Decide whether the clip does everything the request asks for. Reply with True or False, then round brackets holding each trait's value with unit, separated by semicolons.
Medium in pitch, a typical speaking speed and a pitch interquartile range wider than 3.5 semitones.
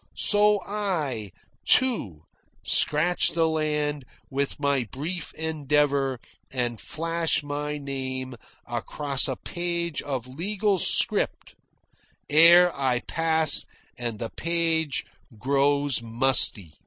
False (145 Hz; 100 wpm; 4.0 semitones)